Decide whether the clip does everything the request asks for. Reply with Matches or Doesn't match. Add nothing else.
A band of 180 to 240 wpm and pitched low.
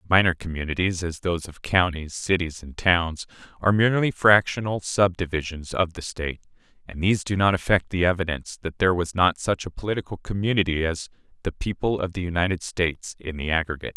Doesn't match